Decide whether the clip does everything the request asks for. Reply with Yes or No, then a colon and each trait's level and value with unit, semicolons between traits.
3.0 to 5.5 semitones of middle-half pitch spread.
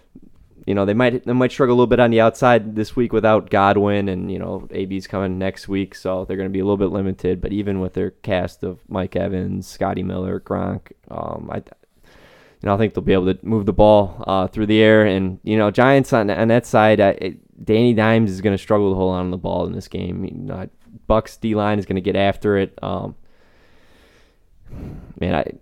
No: narrow, 2.5 semitones